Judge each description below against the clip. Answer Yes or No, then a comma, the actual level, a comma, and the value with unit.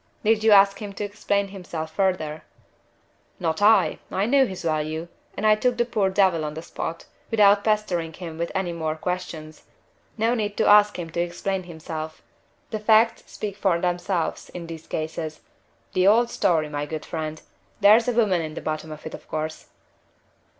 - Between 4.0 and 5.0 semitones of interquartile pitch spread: Yes, average, 4.6 semitones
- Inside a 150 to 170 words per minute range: No, average, 180 wpm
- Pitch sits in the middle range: Yes, medium, 180 Hz